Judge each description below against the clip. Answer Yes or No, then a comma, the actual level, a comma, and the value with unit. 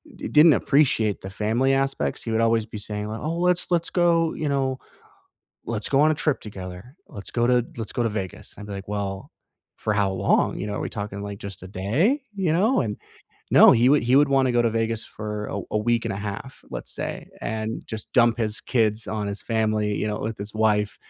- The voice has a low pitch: Yes, low, 110 Hz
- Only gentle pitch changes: No, average, 4.3 semitones